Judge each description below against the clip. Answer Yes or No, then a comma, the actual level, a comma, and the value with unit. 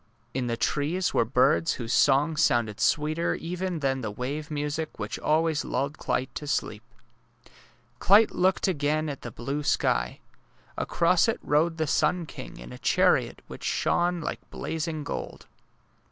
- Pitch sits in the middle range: Yes, medium, 150 Hz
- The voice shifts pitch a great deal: No, average, 3.9 semitones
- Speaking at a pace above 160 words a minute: No, average, 155 wpm